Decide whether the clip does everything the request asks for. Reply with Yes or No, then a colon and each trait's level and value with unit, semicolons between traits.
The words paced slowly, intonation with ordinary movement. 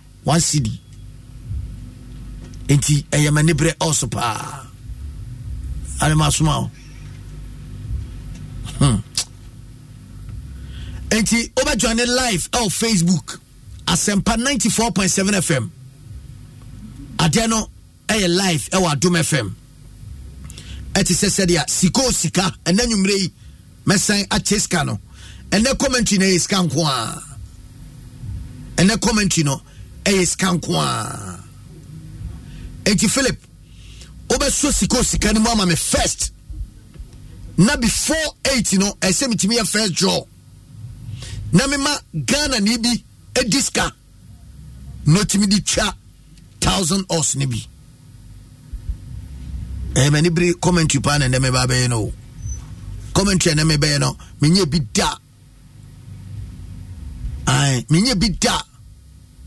No: slow, 100 wpm; wide, 8.8 semitones